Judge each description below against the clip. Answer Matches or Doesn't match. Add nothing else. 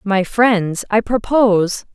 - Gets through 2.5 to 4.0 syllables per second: Matches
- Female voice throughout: Matches